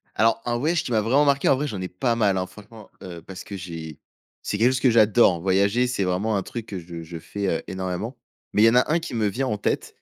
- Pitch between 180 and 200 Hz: No, low, 105 Hz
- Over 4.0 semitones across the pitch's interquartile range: Yes, average, 4.6 semitones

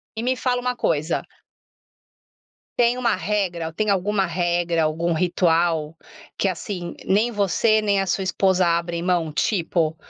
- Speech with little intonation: No, average, 3.6 semitones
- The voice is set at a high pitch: No, medium, 180 Hz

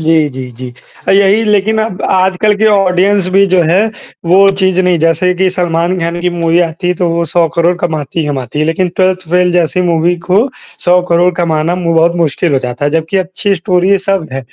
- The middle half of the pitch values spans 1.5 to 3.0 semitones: Yes, narrow, 2.4 semitones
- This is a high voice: No, medium, 175 Hz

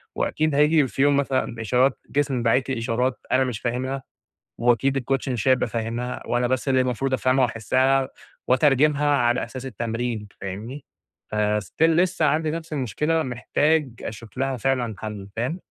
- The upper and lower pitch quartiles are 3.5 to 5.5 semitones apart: No, average, 2.8 semitones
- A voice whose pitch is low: Yes, low, 130 Hz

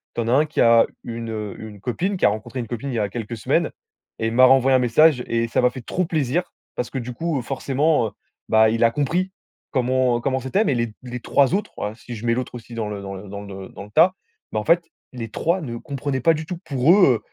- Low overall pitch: Yes, low, 125 Hz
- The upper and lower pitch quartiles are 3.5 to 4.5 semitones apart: Yes, average, 4.0 semitones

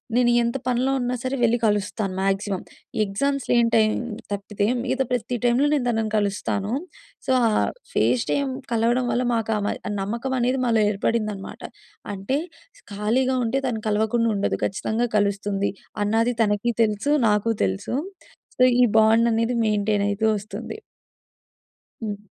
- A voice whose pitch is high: Yes, high, 225 Hz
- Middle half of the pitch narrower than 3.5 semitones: Yes, average, 2.9 semitones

